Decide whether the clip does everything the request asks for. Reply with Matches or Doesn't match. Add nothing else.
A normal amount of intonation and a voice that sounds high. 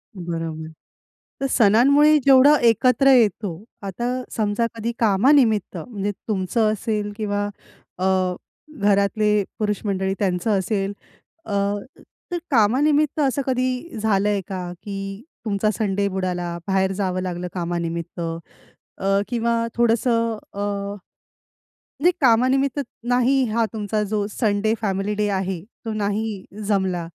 Matches